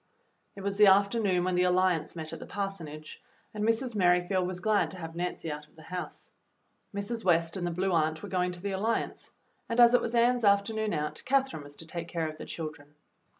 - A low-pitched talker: No, medium, 185 Hz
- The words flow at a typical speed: No, fast, 220 wpm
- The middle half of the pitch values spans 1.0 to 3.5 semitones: No, average, 4.1 semitones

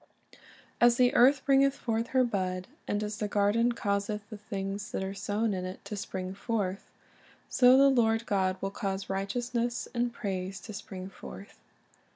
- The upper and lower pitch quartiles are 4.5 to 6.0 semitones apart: No, average, 3.4 semitones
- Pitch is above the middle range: Yes, high, 210 Hz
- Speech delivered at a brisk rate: No, average, 170 wpm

